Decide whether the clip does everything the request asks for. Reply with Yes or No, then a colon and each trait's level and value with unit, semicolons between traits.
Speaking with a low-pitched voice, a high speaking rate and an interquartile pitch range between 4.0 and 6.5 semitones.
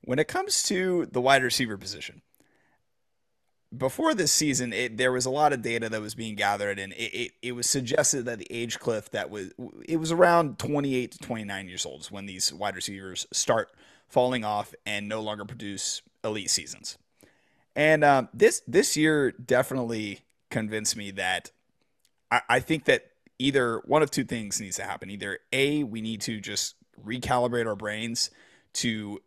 No: low, 120 Hz; average, 180 wpm; average, 4.7 semitones